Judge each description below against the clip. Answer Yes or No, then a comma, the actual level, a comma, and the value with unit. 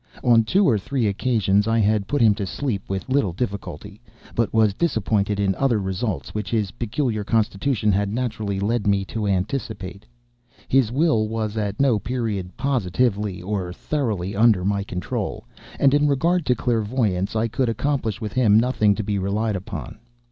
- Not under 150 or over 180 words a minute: Yes, average, 170 wpm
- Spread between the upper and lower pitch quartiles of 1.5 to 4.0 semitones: Yes, average, 3.5 semitones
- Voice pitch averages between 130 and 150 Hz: No, low, 110 Hz